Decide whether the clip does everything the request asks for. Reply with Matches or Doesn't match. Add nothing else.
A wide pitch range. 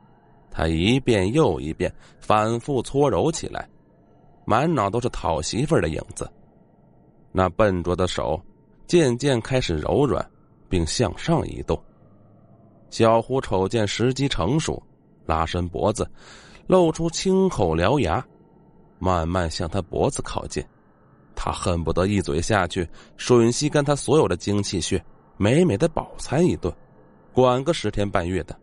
Matches